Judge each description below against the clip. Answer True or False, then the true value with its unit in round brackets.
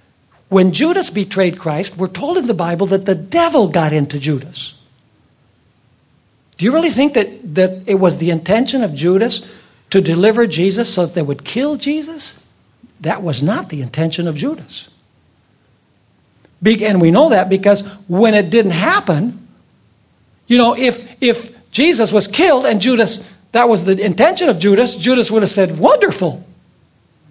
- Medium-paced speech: True (160 wpm)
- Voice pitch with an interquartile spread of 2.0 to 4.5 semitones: False (5.5 semitones)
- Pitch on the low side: False (200 Hz)